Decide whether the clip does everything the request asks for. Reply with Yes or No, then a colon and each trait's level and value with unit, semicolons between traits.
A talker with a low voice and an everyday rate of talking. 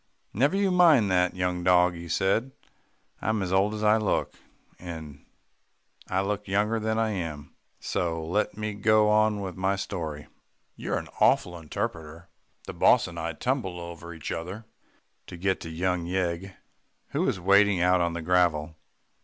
Yes: very low, 90 Hz; average, 165 wpm